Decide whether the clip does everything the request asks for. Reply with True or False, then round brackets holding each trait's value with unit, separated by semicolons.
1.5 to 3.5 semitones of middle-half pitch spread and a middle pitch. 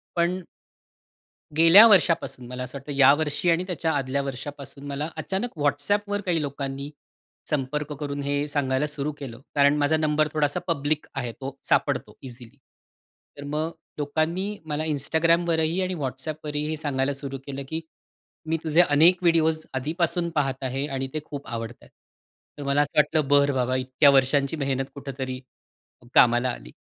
True (2.8 semitones; 145 Hz)